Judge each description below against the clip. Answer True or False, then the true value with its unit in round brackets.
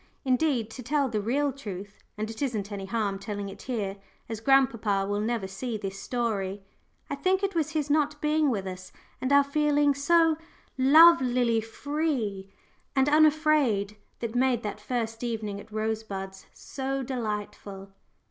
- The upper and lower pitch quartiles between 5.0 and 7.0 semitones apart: True (5.6 semitones)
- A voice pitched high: True (235 Hz)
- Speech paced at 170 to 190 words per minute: False (155 wpm)